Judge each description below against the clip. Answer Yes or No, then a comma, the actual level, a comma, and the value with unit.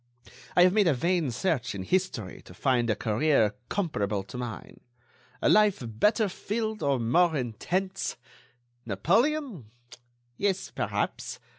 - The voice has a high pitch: No, medium, 155 Hz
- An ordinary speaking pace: No, slow, 130 wpm